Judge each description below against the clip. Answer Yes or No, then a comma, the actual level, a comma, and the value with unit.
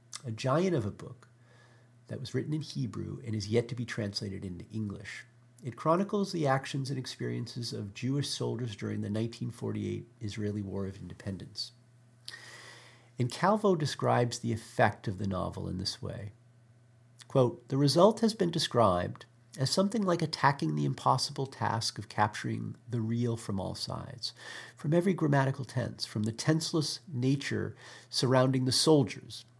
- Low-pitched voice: Yes, low, 120 Hz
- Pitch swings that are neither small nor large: Yes, average, 3.3 semitones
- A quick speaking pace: No, average, 155 wpm